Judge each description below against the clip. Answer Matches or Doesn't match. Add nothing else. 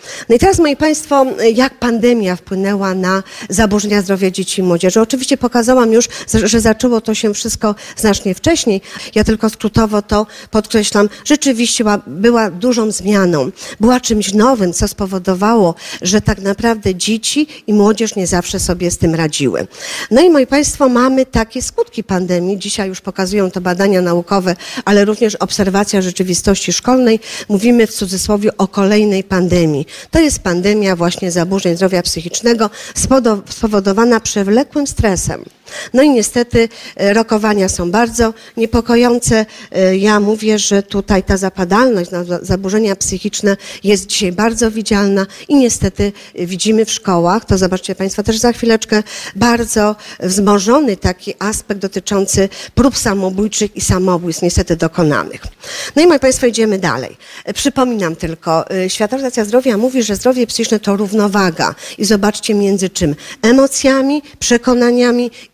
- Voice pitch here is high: Matches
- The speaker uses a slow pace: Doesn't match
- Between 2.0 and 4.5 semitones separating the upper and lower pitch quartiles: Matches